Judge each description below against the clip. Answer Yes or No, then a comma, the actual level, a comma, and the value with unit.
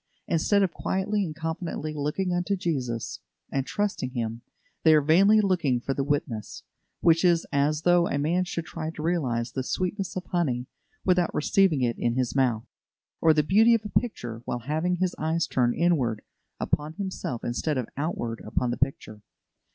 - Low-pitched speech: No, medium, 155 Hz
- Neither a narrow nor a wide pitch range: No, wide, 5.8 semitones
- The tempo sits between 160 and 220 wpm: Yes, average, 175 wpm